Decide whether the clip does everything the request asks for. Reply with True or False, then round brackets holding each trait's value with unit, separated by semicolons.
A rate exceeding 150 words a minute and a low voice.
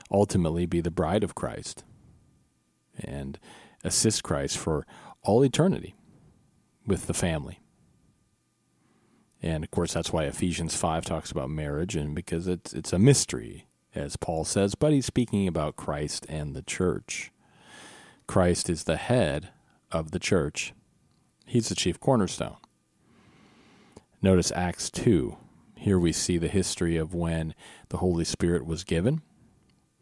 False (135 wpm; 85 Hz)